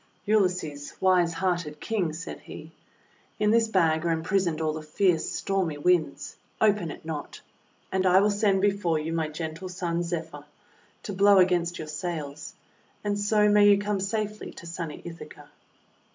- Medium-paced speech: Yes, average, 160 wpm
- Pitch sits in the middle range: Yes, medium, 175 Hz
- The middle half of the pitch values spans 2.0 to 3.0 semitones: No, average, 3.9 semitones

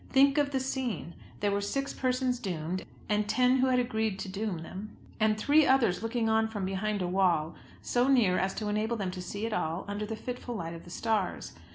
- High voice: Yes, high, 215 Hz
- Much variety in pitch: No, average, 4.7 semitones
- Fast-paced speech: Yes, fast, 220 wpm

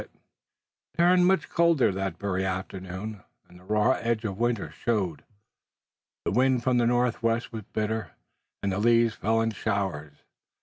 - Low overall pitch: Yes, low, 110 Hz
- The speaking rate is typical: Yes, average, 160 wpm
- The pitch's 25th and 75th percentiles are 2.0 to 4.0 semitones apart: Yes, average, 3.7 semitones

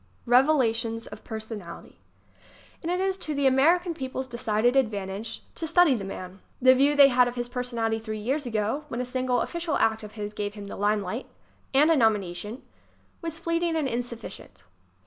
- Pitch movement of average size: Yes, average, 4.5 semitones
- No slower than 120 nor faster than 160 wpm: No, average, 195 wpm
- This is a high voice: Yes, high, 245 Hz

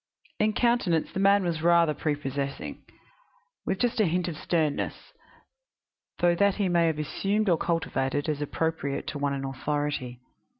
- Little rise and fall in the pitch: No, average, 4.0 semitones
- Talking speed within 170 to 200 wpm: No, average, 155 wpm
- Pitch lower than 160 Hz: No, medium, 165 Hz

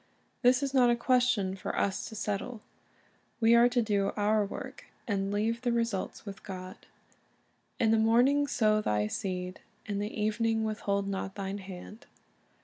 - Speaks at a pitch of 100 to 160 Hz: No, high, 215 Hz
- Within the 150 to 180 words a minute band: Yes, average, 165 wpm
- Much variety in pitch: No, average, 3.0 semitones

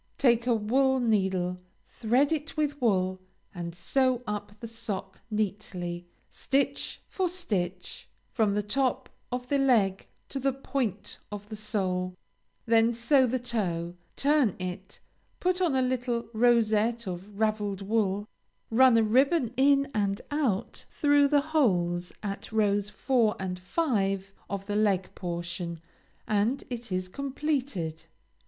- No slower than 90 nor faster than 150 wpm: Yes, slow, 135 wpm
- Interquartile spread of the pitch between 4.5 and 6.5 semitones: Yes, average, 5.2 semitones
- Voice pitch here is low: No, high, 220 Hz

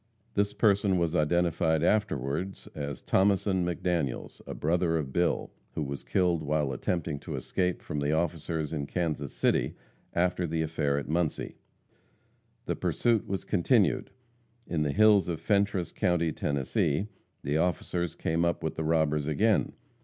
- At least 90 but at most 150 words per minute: Yes, average, 145 wpm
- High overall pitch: No, very low, 85 Hz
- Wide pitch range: No, average, 3.3 semitones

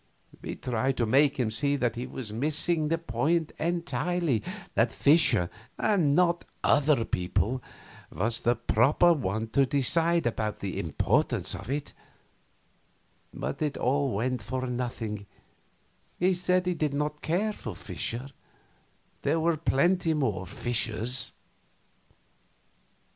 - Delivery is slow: Yes, slow, 125 wpm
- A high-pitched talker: No, low, 135 Hz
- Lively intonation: Yes, wide, 5.8 semitones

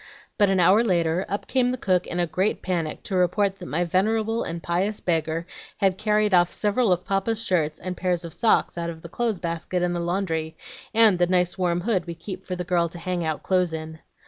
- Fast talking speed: Yes, fast, 225 wpm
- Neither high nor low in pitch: Yes, medium, 180 Hz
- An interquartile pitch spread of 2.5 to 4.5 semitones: Yes, average, 2.8 semitones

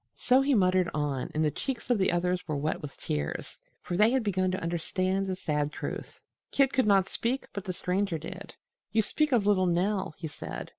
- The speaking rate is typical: No, fast, 210 wpm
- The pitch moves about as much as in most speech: Yes, average, 3.9 semitones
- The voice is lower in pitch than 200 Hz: Yes, medium, 185 Hz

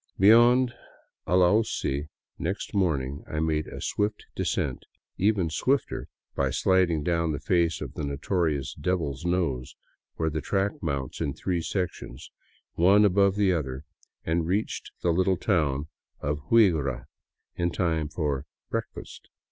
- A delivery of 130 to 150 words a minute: Yes, average, 140 wpm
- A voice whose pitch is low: Yes, very low, 85 Hz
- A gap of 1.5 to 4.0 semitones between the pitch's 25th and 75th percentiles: No, average, 4.4 semitones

